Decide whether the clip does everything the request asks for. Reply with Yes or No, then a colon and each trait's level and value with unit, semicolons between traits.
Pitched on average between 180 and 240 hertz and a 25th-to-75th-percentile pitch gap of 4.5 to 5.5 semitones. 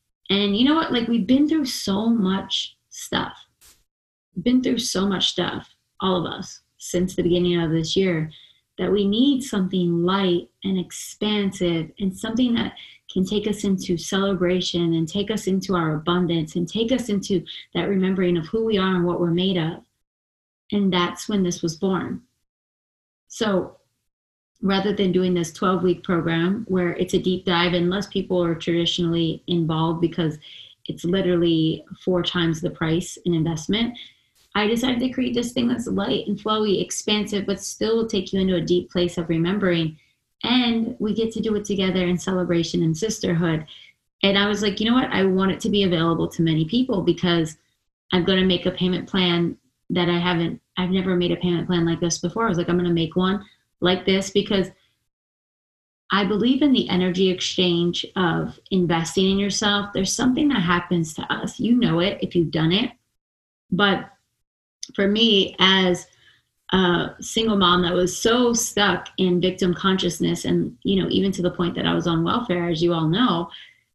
No: medium, 185 Hz; average, 2.9 semitones